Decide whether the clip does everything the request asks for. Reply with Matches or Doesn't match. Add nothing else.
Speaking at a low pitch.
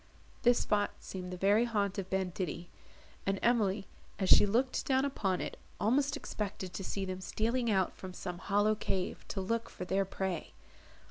Doesn't match